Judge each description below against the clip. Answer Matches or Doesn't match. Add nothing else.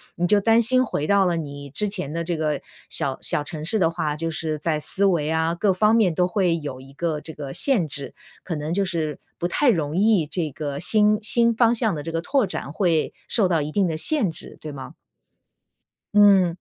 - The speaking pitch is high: Doesn't match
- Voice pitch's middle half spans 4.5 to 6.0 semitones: Matches